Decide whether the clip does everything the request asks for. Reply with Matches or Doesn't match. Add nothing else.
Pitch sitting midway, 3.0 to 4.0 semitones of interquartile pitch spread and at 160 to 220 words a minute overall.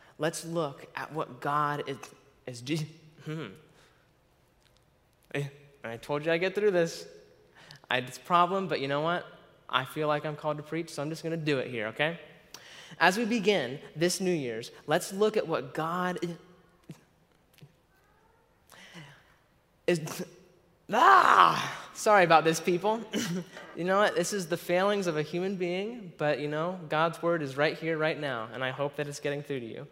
Matches